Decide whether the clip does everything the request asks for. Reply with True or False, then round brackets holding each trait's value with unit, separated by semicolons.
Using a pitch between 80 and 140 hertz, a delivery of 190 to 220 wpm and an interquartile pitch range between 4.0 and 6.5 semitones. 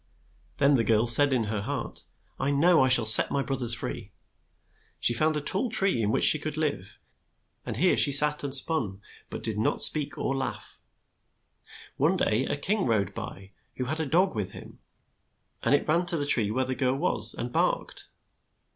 True (135 Hz; 200 wpm; 4.9 semitones)